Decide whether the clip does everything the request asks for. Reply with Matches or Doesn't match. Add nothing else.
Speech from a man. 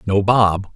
Matches